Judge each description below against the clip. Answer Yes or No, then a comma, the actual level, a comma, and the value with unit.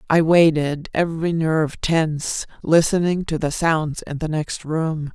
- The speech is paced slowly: No, average, 150 wpm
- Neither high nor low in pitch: Yes, medium, 160 Hz